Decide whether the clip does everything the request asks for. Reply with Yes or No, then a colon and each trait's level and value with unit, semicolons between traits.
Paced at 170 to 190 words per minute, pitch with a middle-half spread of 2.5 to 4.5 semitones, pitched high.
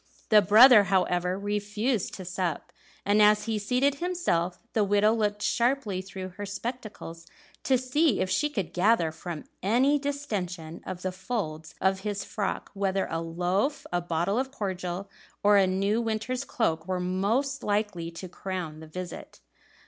No: average, 155 wpm; average, 3.9 semitones; high, 200 Hz